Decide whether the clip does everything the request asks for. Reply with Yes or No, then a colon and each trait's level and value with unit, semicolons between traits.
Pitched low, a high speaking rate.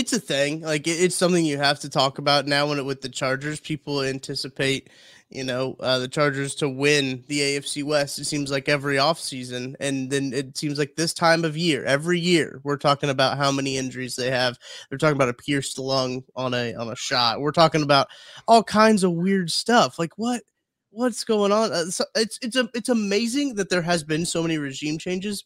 No: medium, 145 Hz; fast, 215 wpm